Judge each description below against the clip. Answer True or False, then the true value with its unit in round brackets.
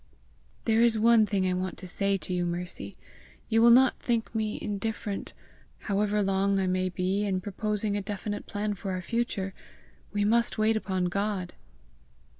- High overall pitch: True (205 Hz)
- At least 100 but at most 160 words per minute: False (170 wpm)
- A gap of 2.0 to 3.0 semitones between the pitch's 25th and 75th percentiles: True (2.6 semitones)